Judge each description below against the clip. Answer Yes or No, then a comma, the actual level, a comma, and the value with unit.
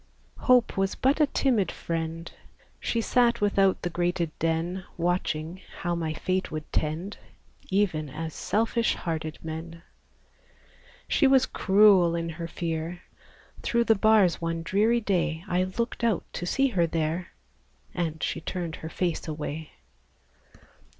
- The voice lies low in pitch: No, medium, 175 Hz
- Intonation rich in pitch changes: No, average, 4.1 semitones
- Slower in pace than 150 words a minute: Yes, slow, 135 wpm